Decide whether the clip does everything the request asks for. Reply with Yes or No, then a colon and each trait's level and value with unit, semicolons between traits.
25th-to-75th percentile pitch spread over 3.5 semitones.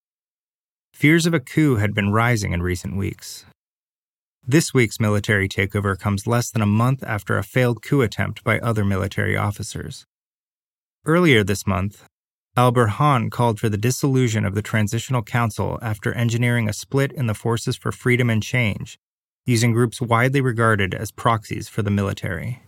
No: average, 3.0 semitones